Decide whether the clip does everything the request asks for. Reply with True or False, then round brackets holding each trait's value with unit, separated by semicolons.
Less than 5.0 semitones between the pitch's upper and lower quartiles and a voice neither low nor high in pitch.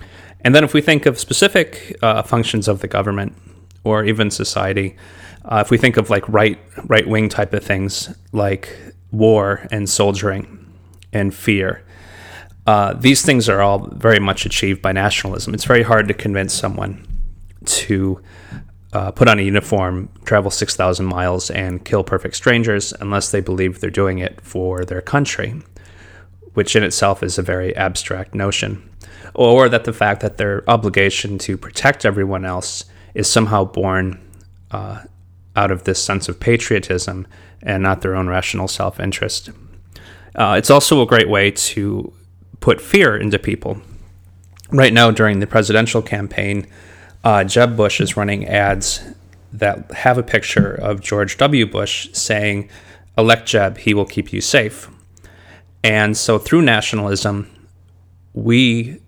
False (2.8 semitones; 100 Hz)